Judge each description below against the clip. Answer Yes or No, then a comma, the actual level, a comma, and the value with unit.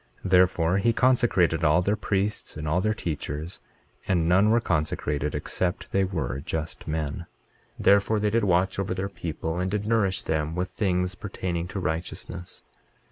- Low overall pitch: Yes, very low, 90 Hz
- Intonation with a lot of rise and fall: No, average, 3.4 semitones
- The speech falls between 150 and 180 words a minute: Yes, average, 165 wpm